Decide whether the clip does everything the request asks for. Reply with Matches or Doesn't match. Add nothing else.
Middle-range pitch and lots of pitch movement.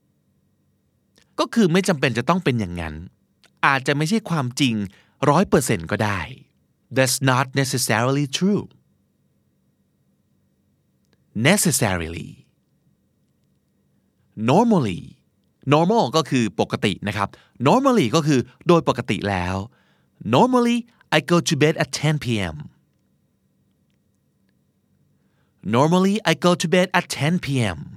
Matches